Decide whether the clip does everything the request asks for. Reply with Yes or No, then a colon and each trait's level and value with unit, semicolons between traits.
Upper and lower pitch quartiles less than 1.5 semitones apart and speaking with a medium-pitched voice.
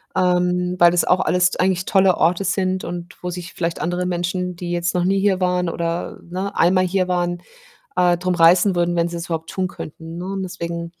Yes: narrow, 1.1 semitones; medium, 180 Hz